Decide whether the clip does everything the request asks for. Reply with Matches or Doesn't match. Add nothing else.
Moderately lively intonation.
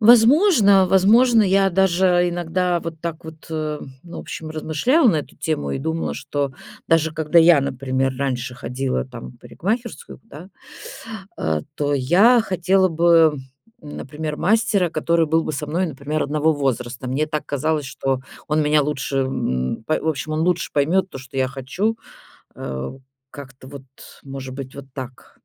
Matches